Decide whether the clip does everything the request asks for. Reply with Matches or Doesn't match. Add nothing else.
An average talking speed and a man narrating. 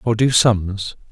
Matches